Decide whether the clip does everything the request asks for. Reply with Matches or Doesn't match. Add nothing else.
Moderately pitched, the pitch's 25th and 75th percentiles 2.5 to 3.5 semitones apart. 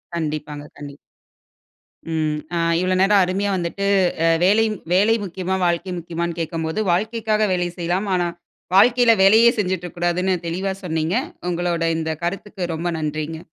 Matches